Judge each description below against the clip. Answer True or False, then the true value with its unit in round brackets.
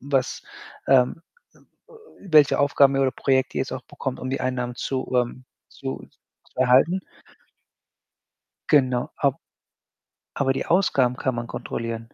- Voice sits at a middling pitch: False (130 Hz)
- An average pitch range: False (1.8 semitones)